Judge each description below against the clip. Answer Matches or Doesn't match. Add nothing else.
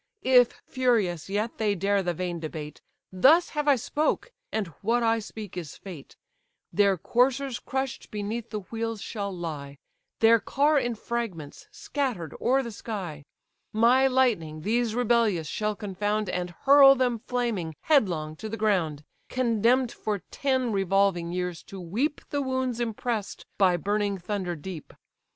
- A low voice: Doesn't match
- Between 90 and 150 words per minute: Matches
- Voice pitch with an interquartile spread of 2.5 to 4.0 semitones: Doesn't match